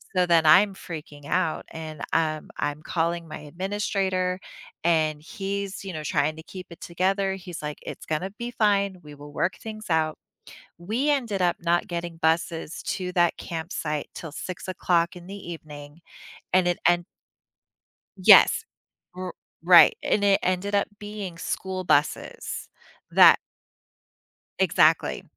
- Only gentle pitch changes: No, average, 3.2 semitones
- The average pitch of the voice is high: No, medium, 175 Hz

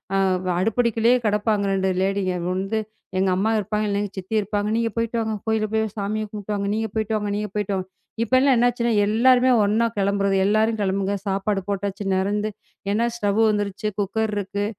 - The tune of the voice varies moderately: No, narrow, 1.8 semitones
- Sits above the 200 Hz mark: Yes, high, 210 Hz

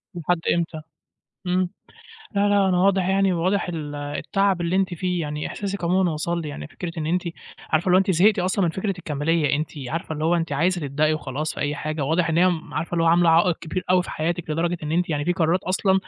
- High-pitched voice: No, medium, 170 Hz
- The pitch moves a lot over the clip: No, average, 2.8 semitones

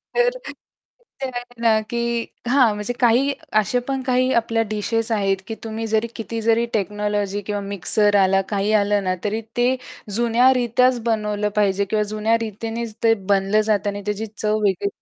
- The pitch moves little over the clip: Yes, narrow, 2.3 semitones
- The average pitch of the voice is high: Yes, high, 220 Hz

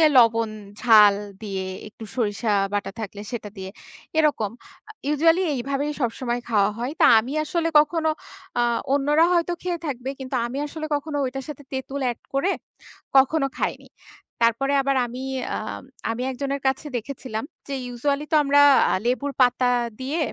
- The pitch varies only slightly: No, average, 3.8 semitones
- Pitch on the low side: No, very high, 265 Hz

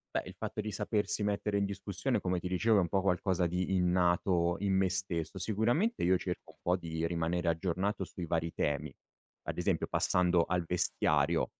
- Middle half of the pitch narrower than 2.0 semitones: No, narrow, 2.6 semitones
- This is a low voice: Yes, very low, 90 Hz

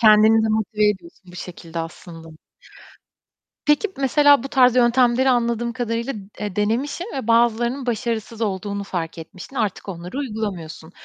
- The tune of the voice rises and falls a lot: No, average, 4.1 semitones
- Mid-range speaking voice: No, high, 220 Hz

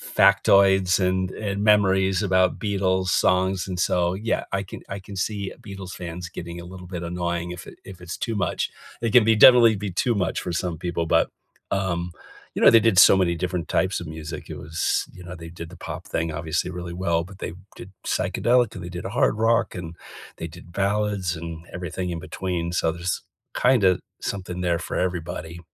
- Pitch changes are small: Yes, narrow, 2.3 semitones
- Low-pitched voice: Yes, very low, 90 Hz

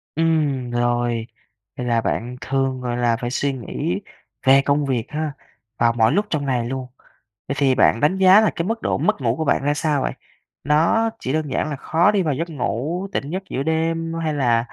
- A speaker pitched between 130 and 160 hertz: Yes, medium, 140 Hz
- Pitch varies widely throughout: No, average, 4.7 semitones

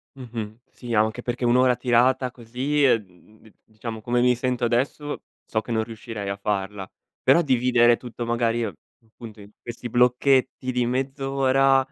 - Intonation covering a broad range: No, narrow, 2.4 semitones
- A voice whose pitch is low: Yes, low, 120 Hz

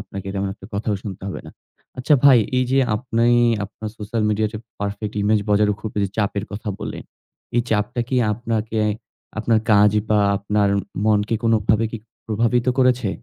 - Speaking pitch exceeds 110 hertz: No, low, 105 Hz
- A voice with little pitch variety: Yes, narrow, 1.9 semitones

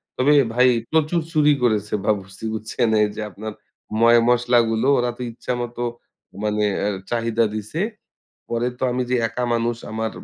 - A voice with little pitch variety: Yes, narrow, 2.2 semitones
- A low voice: Yes, low, 115 Hz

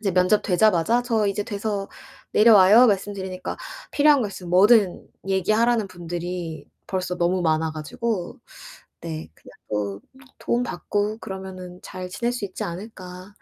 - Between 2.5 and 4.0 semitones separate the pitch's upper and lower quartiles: Yes, average, 3.2 semitones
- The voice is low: No, high, 190 Hz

